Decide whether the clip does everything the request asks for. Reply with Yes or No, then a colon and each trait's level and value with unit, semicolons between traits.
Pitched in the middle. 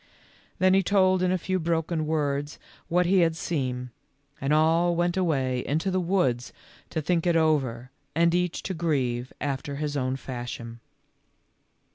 Yes: medium, 160 Hz